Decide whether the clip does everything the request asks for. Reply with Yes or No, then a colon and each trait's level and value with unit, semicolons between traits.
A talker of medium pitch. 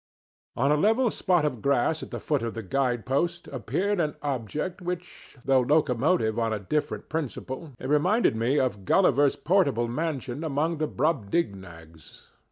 Yes: medium, 145 Hz